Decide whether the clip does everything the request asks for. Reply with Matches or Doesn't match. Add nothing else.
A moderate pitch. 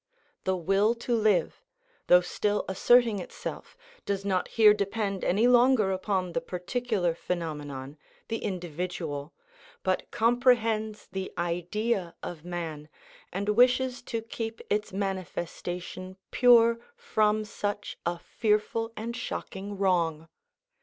Doesn't match